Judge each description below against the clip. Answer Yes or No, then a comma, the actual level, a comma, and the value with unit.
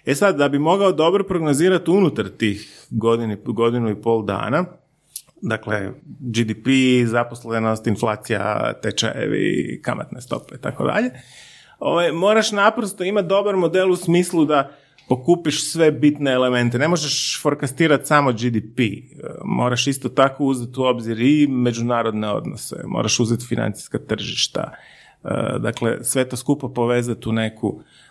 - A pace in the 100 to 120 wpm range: No, average, 130 wpm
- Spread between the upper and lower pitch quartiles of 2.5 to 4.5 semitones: No, average, 5.0 semitones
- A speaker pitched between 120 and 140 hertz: Yes, low, 130 Hz